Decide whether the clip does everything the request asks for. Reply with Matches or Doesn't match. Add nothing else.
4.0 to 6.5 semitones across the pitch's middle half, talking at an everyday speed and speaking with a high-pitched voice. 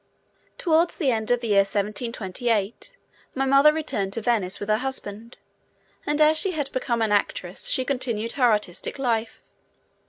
Matches